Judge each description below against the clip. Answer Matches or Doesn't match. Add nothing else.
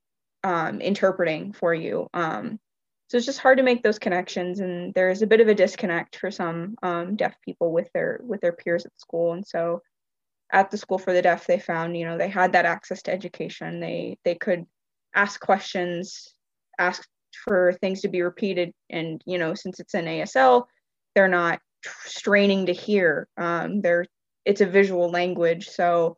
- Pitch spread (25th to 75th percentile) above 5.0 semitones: Doesn't match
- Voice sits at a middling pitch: Matches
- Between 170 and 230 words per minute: Matches